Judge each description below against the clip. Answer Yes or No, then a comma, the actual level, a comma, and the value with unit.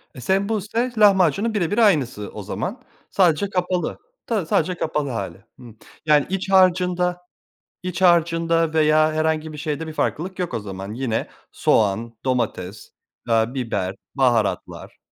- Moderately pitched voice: Yes, medium, 160 Hz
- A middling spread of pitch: No, wide, 7.1 semitones